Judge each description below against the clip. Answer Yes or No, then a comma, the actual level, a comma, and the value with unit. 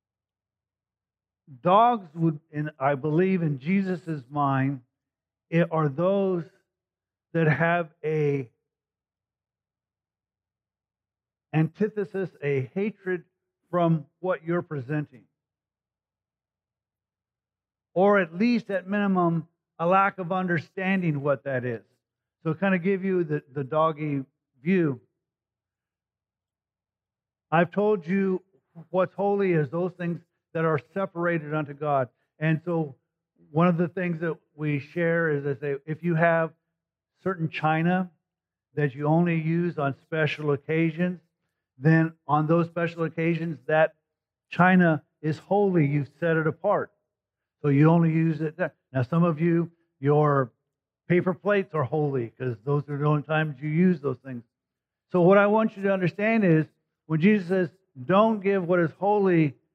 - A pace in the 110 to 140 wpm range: Yes, slow, 135 wpm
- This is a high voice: No, medium, 160 Hz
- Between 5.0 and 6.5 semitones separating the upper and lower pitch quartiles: No, average, 4.2 semitones